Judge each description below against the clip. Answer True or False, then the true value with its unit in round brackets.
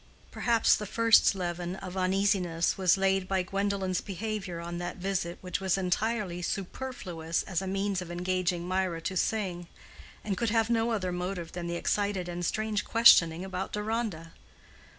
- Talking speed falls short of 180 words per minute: True (160 wpm)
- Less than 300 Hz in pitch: True (190 Hz)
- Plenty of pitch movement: False (2.6 semitones)